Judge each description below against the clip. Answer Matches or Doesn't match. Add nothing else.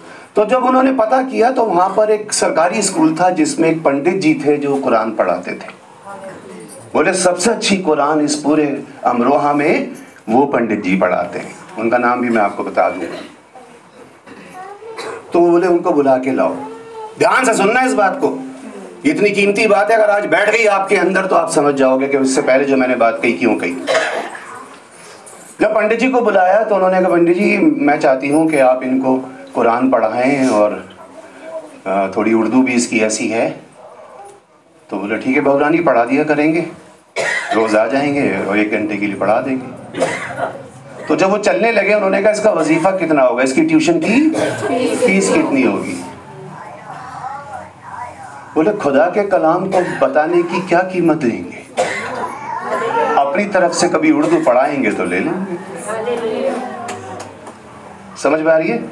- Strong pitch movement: Matches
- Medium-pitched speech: Matches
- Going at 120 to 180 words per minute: Matches